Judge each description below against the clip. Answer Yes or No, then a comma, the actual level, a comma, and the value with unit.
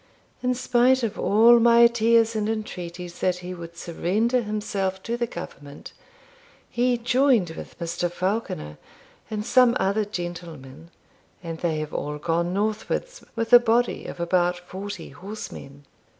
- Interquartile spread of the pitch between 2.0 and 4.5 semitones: No, average, 5.3 semitones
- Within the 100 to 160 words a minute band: Yes, average, 140 wpm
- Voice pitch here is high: Yes, high, 200 Hz